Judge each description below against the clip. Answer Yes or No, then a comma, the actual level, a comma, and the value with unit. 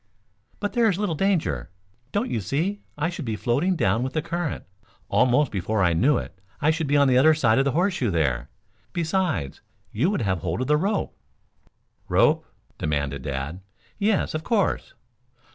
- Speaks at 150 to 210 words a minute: Yes, average, 180 wpm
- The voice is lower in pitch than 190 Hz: Yes, medium, 140 Hz